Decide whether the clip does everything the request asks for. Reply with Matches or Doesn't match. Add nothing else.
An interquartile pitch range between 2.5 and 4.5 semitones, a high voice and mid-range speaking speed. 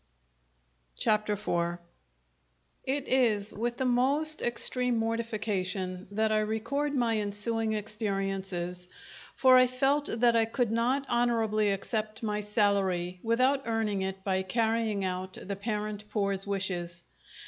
Doesn't match